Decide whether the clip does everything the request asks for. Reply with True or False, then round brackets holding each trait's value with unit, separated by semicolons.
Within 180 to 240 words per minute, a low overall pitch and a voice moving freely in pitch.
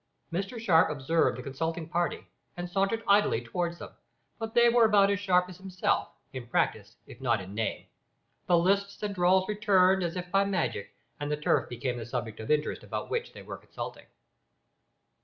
False (185 wpm; 175 Hz; 6.9 semitones)